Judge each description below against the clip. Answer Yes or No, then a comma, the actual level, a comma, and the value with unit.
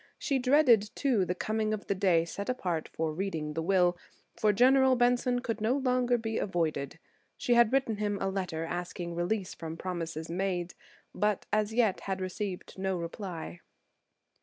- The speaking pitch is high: Yes, high, 195 Hz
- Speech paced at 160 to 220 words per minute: Yes, average, 170 wpm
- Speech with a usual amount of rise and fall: Yes, average, 4.9 semitones